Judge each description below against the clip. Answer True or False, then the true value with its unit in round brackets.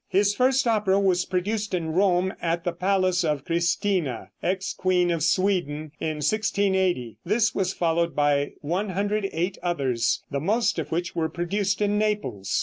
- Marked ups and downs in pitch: False (3.5 semitones)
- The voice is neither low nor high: True (180 Hz)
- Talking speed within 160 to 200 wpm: False (150 wpm)